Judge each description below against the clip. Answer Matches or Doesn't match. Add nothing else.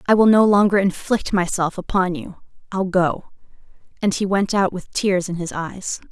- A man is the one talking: Doesn't match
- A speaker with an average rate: Matches